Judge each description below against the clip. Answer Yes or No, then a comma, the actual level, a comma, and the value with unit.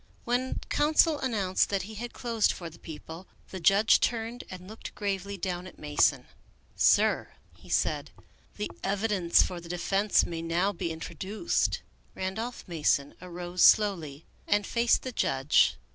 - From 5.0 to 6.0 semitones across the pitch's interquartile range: No, average, 4.3 semitones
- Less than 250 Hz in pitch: Yes, high, 190 Hz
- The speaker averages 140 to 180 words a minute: Yes, average, 155 wpm